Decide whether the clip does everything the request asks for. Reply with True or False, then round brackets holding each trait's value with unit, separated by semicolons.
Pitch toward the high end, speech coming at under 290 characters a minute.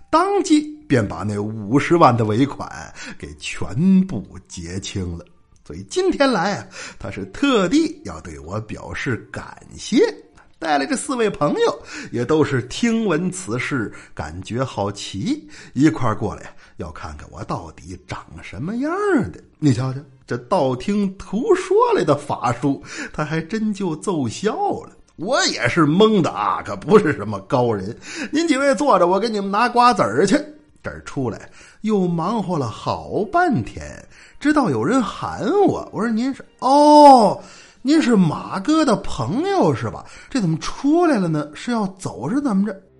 True (195 Hz; 225 characters per minute)